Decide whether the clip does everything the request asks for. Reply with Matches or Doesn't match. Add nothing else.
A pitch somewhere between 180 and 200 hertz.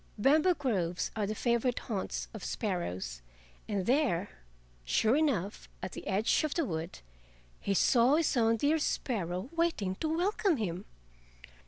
Doesn't match